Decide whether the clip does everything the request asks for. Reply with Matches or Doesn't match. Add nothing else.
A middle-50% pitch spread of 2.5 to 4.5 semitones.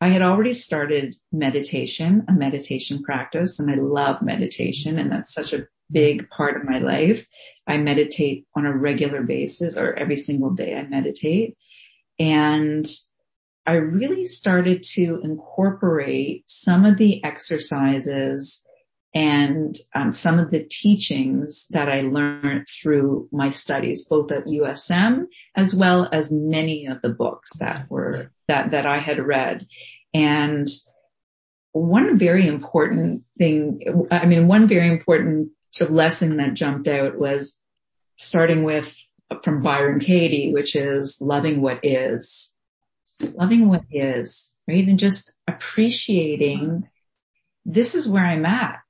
Matches